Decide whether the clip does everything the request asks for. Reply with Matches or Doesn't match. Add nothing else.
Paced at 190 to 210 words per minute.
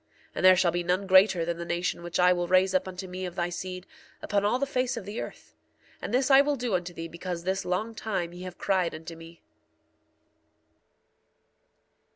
Matches